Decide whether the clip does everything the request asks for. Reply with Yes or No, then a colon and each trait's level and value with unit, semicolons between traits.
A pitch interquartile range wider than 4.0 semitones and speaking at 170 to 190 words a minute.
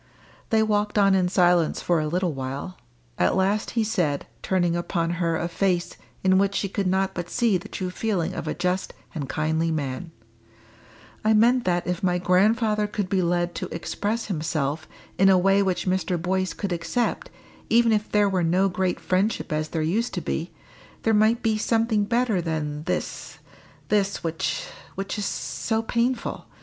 No: average, 3.6 semitones; average, 180 wpm